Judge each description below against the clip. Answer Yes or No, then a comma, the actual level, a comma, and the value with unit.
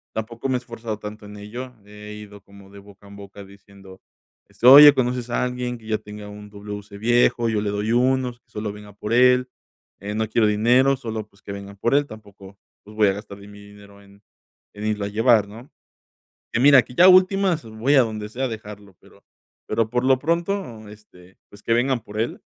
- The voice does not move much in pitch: No, average, 3.2 semitones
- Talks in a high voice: No, low, 110 Hz